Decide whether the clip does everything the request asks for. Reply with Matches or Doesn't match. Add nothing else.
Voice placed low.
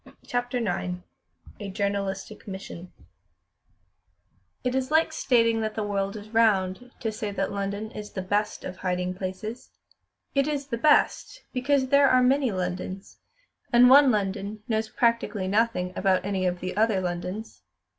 Doesn't match